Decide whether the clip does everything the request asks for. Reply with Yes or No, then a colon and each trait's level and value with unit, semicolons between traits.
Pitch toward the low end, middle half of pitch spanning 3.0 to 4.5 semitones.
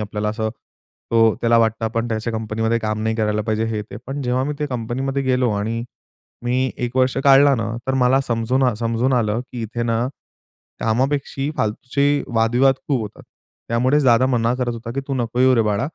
No: low, 120 Hz; narrow, 2.6 semitones